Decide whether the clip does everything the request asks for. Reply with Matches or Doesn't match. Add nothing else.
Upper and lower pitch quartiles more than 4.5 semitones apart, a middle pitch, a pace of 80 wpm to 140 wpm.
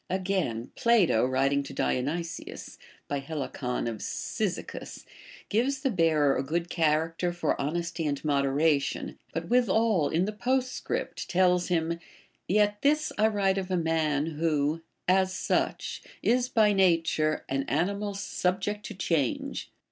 Matches